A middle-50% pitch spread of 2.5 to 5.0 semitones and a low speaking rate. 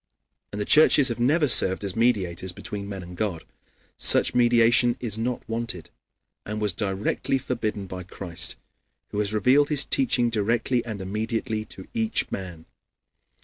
No: average, 4.0 semitones; average, 150 wpm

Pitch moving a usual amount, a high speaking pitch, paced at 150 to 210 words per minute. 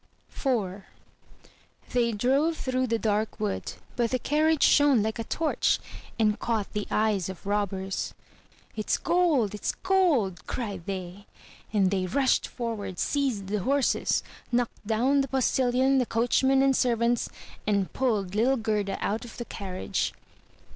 No: average, 4.5 semitones; high, 230 Hz; average, 140 wpm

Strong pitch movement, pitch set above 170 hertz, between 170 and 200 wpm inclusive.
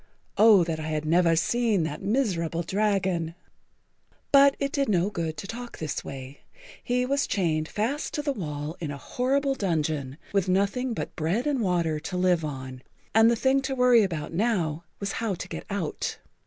Yes: wide, 6.8 semitones; medium, 185 Hz; average, 180 wpm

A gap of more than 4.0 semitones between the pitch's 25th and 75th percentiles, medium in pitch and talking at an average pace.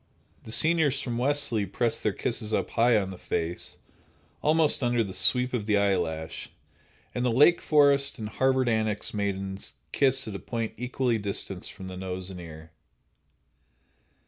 No: average, 5.0 semitones; low, 110 Hz; average, 160 wpm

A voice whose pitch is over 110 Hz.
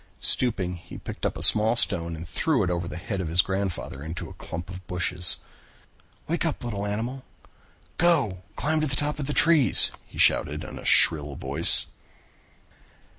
No: low, 100 Hz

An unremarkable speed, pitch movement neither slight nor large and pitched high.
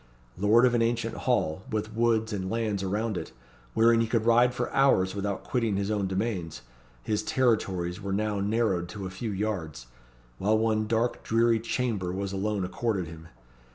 No: average, 175 wpm; average, 3.2 semitones; low, 105 Hz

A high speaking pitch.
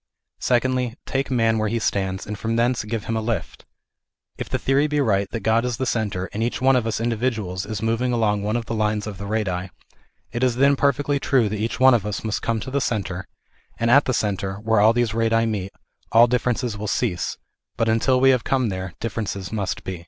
No: low, 115 Hz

